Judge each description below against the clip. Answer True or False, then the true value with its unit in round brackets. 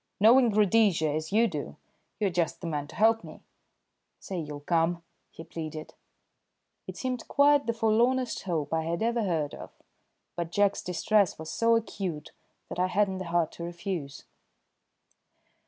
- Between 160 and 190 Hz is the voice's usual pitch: True (185 Hz)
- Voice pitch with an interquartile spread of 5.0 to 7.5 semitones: True (5.4 semitones)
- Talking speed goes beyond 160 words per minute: False (155 wpm)